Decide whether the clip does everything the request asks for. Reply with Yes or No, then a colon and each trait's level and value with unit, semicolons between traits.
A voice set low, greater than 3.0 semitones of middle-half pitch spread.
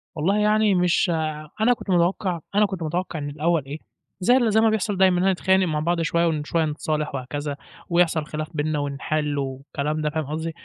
No: medium, 165 Hz; average, 3.7 semitones